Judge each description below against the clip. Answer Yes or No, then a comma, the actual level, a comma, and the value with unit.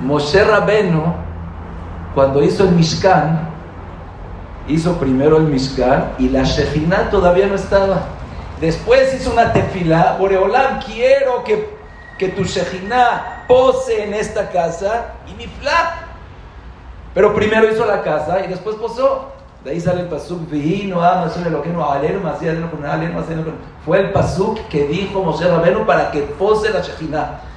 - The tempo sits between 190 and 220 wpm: No, slow, 135 wpm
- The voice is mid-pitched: Yes, medium, 180 Hz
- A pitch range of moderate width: No, wide, 5.7 semitones